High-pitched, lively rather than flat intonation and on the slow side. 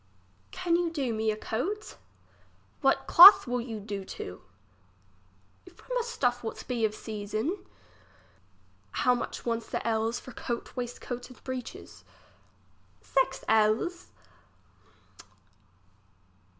Yes: high, 245 Hz; wide, 5.7 semitones; slow, 115 wpm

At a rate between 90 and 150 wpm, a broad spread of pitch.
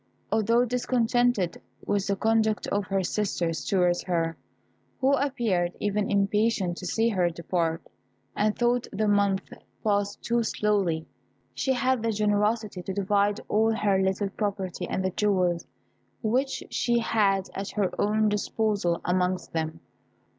No: average, 140 wpm; average, 3.0 semitones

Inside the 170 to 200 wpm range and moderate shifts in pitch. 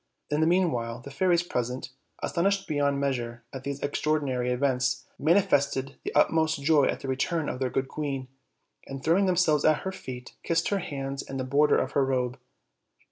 Yes: average, 185 wpm; average, 3.5 semitones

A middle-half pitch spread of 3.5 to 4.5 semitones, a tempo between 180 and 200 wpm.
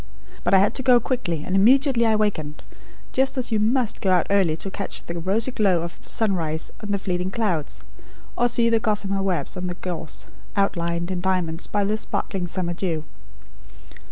Yes: average, 4.1 semitones; average, 190 wpm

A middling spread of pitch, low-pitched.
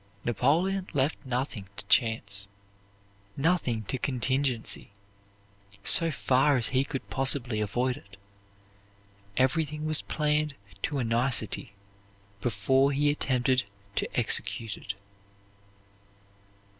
Yes: average, 3.9 semitones; low, 130 Hz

